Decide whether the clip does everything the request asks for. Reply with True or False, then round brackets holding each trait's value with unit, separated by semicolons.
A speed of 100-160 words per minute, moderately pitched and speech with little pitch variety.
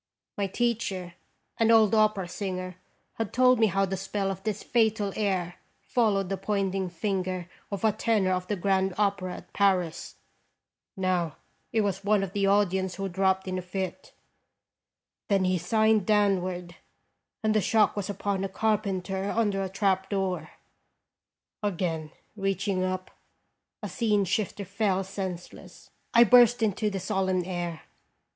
False (150 wpm; 195 Hz; 2.1 semitones)